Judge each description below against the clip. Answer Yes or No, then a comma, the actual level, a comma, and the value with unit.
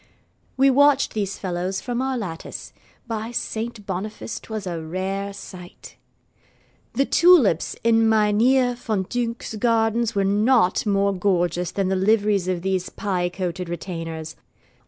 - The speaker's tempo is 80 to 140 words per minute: Yes, slow, 135 wpm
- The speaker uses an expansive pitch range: No, average, 3.9 semitones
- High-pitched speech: Yes, high, 200 Hz